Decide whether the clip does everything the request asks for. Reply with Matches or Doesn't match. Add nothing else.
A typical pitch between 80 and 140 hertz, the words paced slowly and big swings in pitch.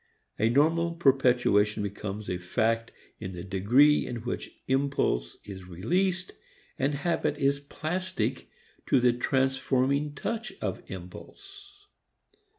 Matches